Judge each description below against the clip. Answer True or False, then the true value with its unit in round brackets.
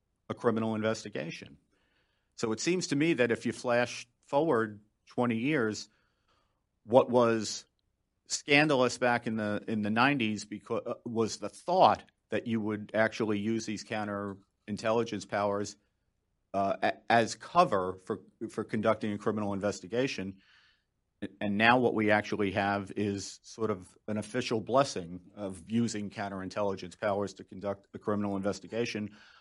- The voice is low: True (105 Hz)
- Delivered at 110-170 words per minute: True (140 wpm)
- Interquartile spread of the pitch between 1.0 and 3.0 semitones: True (2.5 semitones)